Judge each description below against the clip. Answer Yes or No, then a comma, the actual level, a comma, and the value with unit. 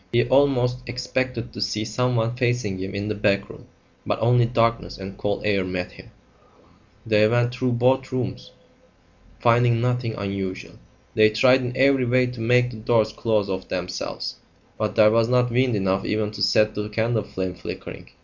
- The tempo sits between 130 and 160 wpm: No, average, 175 wpm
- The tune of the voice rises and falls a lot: No, average, 2.9 semitones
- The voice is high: No, low, 115 Hz